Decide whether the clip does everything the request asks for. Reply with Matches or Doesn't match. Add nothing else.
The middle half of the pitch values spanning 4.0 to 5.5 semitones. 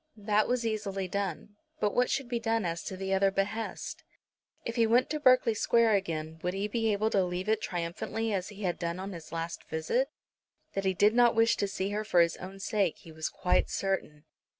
Doesn't match